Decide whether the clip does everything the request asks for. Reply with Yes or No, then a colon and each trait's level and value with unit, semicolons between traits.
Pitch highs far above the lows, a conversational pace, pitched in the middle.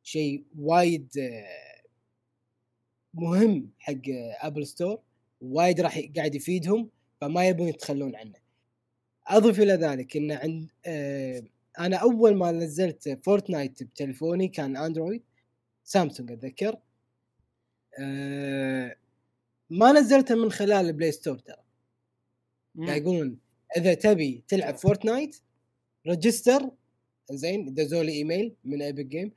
Yes: wide, 6.5 semitones; average, 100 wpm; medium, 150 Hz